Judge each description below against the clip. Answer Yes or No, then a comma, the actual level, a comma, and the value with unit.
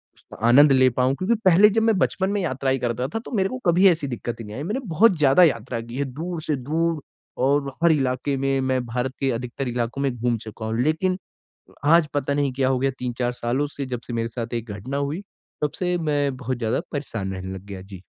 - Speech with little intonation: No, average, 4.7 semitones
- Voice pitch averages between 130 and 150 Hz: Yes, low, 135 Hz